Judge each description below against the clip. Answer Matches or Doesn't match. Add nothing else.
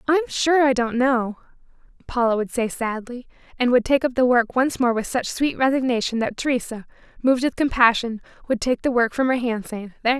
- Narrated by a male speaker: Doesn't match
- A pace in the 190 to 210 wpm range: Matches